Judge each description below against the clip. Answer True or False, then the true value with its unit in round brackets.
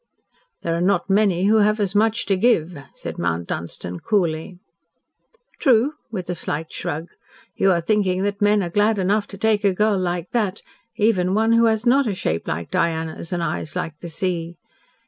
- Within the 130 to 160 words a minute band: False (185 wpm)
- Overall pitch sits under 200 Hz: True (190 Hz)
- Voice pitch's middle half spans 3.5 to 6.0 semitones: True (4.0 semitones)